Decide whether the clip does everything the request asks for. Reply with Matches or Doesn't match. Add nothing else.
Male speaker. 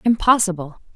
Doesn't match